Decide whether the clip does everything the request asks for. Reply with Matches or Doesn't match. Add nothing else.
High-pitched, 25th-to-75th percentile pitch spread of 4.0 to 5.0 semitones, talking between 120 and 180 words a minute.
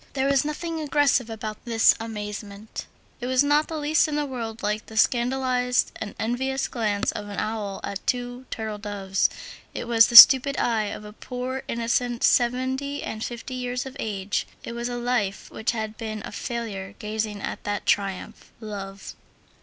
Doesn't match